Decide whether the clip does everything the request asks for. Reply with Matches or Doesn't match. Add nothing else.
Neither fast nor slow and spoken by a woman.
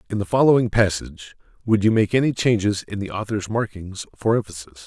Doesn't match